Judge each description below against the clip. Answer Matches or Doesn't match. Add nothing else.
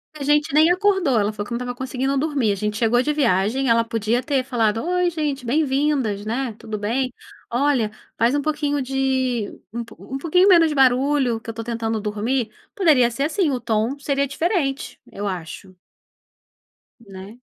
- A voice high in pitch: Matches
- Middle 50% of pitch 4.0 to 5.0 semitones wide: Matches